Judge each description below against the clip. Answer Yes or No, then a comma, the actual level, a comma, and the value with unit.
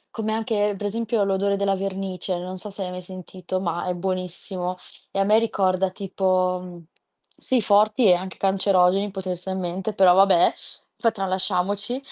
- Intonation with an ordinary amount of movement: No, narrow, 1.8 semitones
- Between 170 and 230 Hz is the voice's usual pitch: Yes, high, 190 Hz